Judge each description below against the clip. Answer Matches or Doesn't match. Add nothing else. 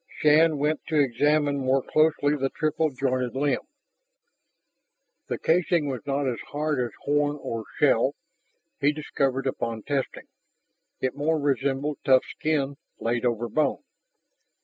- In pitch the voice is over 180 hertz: Doesn't match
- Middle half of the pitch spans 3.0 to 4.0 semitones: Doesn't match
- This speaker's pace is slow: Matches